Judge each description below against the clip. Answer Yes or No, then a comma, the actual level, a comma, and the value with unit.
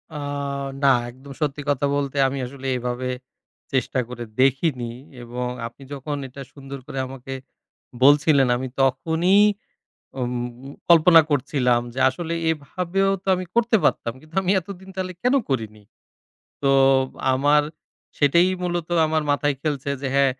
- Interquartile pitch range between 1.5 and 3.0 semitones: No, average, 3.8 semitones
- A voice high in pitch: No, medium, 140 Hz